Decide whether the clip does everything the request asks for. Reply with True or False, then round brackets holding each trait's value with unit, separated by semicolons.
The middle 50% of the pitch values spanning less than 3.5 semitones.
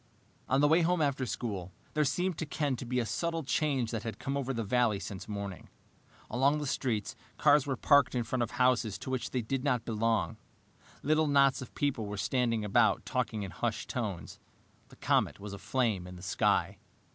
False (4.9 semitones)